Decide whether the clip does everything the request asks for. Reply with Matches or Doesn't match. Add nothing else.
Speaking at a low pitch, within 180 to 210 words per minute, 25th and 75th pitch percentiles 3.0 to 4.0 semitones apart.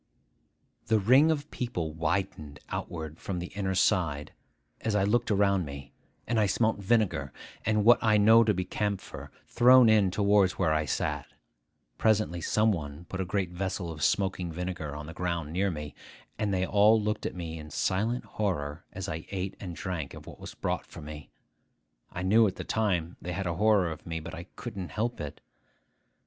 Doesn't match